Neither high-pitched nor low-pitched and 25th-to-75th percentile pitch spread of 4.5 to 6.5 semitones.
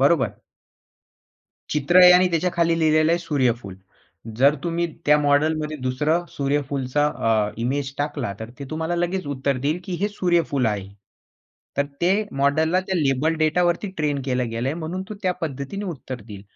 No: medium, 150 Hz; average, 4.0 semitones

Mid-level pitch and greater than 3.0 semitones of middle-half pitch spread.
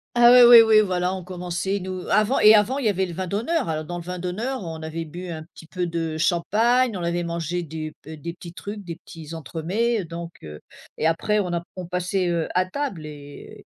Yes: medium, 180 Hz; average, 3.7 semitones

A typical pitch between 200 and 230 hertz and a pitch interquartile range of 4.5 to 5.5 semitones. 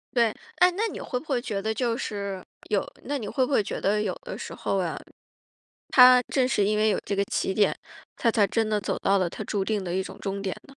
No: high, 215 Hz; average, 4.1 semitones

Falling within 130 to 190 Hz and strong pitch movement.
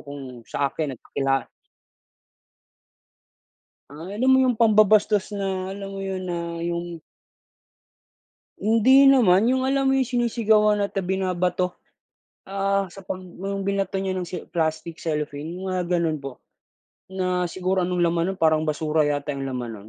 No: medium, 185 Hz; average, 3.8 semitones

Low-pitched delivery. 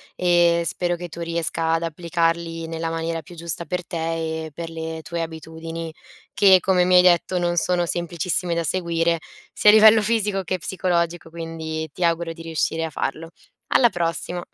No: medium, 170 Hz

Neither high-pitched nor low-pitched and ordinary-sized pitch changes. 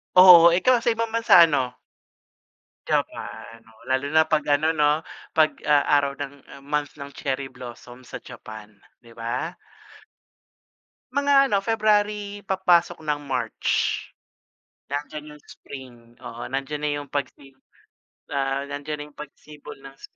Yes: medium, 150 Hz; average, 4.8 semitones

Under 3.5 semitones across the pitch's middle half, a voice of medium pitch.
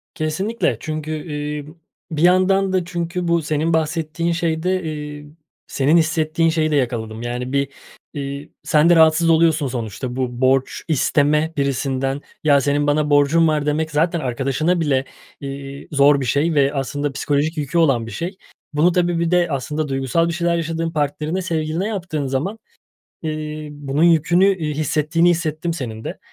Yes: average, 3.0 semitones; medium, 155 Hz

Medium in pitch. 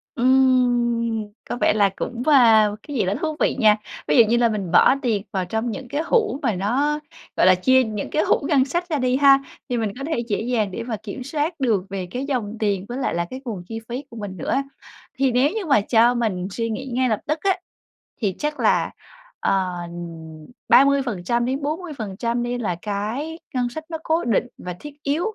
No: high, 240 Hz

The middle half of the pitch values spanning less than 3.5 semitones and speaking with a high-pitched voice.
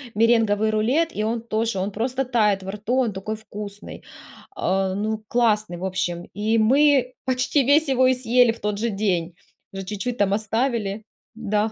Yes: average, 3.1 semitones; high, 220 Hz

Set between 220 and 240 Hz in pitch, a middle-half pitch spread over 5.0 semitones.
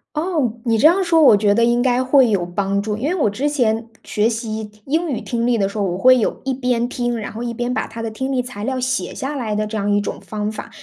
No: high, 235 Hz; average, 3.4 semitones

